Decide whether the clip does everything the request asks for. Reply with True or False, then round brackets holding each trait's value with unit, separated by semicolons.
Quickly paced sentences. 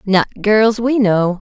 False (165 wpm)